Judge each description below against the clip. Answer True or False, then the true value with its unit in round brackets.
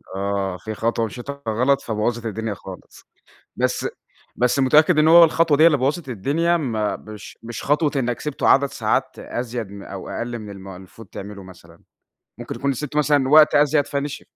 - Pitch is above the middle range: False (120 Hz)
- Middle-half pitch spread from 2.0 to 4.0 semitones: False (5.4 semitones)